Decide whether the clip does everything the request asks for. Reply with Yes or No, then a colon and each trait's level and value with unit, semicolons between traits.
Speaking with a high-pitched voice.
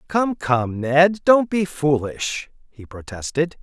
No: medium, 155 Hz